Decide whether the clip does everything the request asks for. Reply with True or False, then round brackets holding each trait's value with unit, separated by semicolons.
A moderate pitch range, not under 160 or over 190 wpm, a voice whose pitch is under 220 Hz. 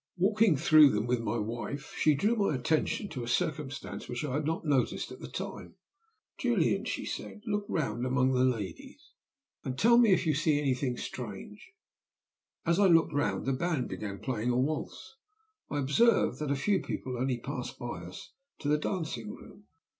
True (4.7 semitones; 185 wpm; 140 Hz)